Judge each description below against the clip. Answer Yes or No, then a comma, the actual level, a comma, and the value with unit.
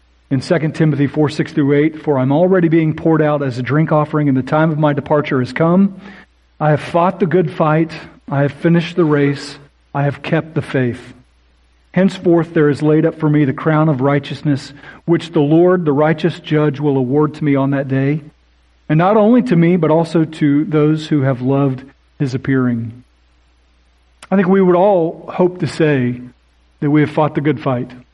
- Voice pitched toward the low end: No, medium, 150 Hz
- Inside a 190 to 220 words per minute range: Yes, average, 200 wpm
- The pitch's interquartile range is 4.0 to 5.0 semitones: No, average, 3.2 semitones